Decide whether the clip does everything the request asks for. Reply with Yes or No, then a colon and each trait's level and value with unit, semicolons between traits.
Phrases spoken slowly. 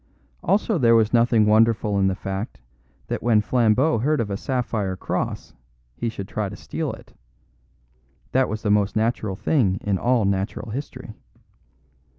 No: average, 160 wpm